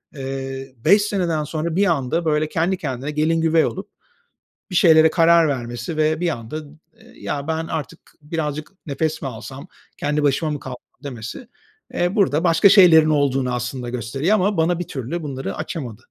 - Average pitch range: Yes, average, 3.6 semitones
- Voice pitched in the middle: Yes, medium, 155 Hz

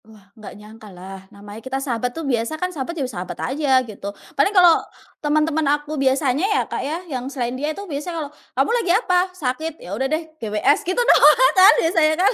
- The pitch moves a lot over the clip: Yes, wide, 6.1 semitones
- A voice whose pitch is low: No, very high, 280 Hz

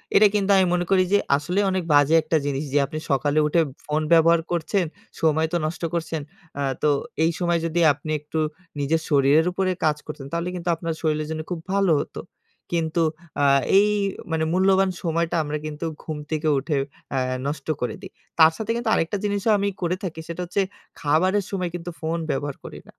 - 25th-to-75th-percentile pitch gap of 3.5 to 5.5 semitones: No, average, 3.0 semitones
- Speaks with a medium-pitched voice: Yes, medium, 165 Hz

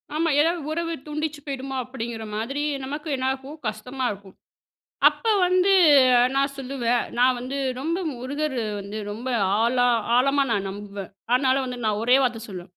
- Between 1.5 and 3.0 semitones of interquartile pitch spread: No, average, 4.1 semitones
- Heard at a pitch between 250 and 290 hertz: Yes, very high, 260 Hz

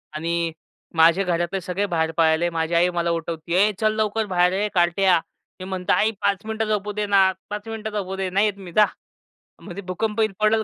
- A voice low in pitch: No, high, 190 Hz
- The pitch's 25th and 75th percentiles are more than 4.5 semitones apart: No, average, 3.6 semitones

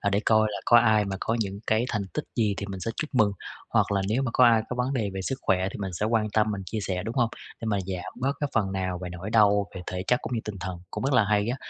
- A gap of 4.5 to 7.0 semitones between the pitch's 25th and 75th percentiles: No, average, 3.0 semitones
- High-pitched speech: No, low, 105 Hz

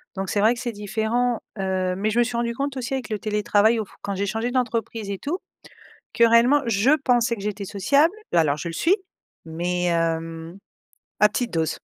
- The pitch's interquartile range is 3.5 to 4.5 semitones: Yes, average, 4.0 semitones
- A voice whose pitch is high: Yes, high, 215 Hz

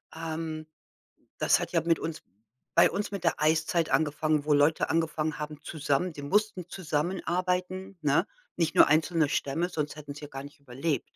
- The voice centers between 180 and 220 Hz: No, medium, 160 Hz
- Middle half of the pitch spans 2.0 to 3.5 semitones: Yes, narrow, 2.6 semitones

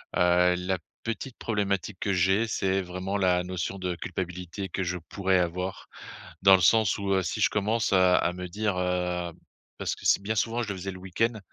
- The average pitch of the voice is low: Yes, very low, 95 Hz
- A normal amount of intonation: No, narrow, 2.0 semitones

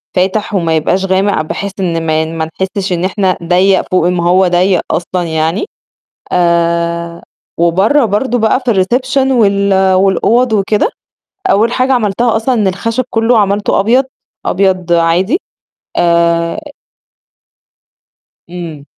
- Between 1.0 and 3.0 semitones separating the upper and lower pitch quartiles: No, average, 4.1 semitones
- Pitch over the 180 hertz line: Yes, high, 190 Hz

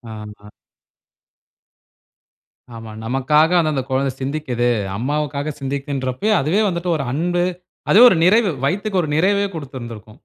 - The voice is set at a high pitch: No, medium, 145 Hz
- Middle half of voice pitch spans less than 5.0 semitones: No, average, 5.3 semitones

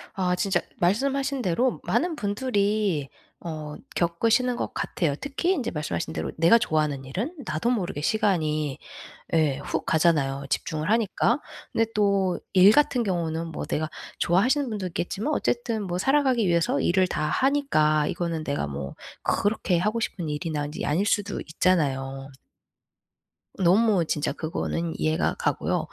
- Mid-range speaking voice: Yes, medium, 180 Hz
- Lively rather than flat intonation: Yes, wide, 6.6 semitones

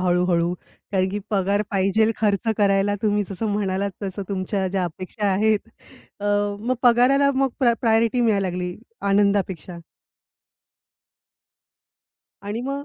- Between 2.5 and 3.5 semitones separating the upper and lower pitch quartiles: Yes, average, 2.8 semitones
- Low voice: No, high, 200 Hz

